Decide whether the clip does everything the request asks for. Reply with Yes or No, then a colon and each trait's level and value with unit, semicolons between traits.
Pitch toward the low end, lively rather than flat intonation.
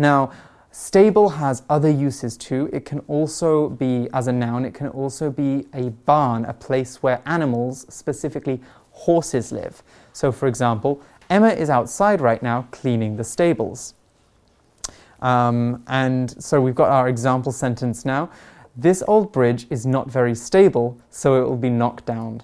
No: low, 130 Hz; average, 3.3 semitones